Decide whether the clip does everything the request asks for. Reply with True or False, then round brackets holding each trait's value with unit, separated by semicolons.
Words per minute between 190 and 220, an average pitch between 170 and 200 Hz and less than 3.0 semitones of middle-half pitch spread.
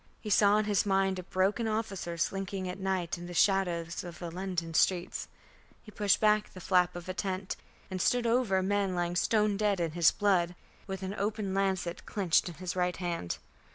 True (200 wpm; 190 Hz; 2.5 semitones)